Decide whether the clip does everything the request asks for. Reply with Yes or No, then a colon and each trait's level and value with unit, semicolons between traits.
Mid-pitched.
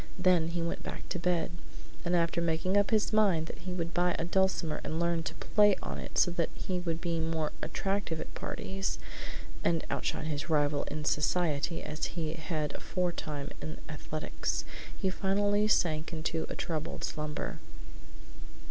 Yes: medium, 170 Hz